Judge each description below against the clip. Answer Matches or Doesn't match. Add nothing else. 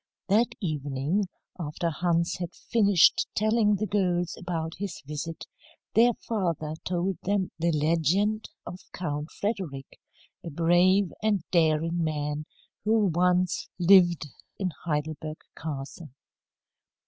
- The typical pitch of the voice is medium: Matches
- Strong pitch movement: Doesn't match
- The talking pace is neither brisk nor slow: Doesn't match